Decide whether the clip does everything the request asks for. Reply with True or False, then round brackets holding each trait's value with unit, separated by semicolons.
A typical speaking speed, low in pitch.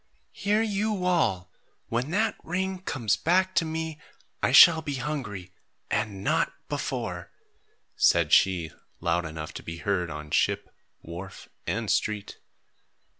False (130 wpm; 120 Hz)